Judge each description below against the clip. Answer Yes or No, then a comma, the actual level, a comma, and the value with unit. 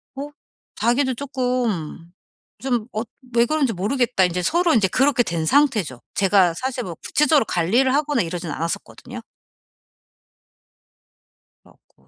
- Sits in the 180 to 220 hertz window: No, high, 235 Hz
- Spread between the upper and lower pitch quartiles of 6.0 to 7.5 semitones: Yes, wide, 7.0 semitones